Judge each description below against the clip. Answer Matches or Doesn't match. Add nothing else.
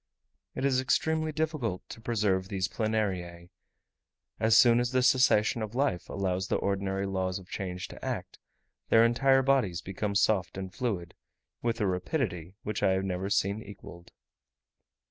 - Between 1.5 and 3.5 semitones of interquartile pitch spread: Doesn't match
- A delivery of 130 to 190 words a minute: Matches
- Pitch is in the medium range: Doesn't match